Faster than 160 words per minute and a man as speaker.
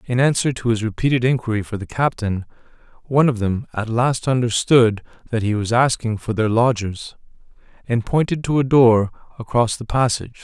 Yes: average, 170 wpm; male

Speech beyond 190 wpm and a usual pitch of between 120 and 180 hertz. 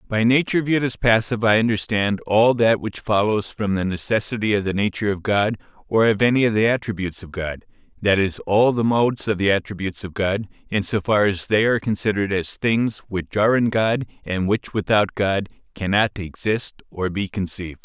No: average, 200 wpm; low, 105 Hz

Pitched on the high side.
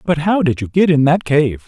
No: medium, 155 Hz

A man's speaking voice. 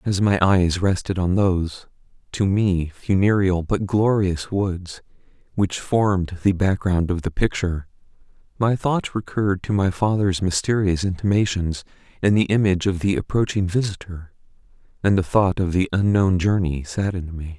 Yes: male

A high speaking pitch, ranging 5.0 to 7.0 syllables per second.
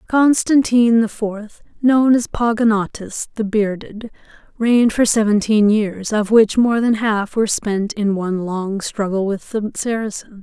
No: high, 215 Hz; 4.4 syllables/s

